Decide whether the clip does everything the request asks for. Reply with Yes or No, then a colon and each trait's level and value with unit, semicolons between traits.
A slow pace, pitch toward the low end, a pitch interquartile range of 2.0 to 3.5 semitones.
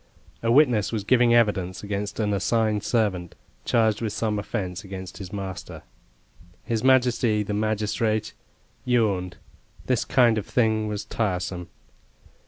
Yes: slow, 130 wpm; low, 105 Hz; average, 2.8 semitones